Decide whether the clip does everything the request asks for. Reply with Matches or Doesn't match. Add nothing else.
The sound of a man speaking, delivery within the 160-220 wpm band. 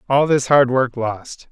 Matches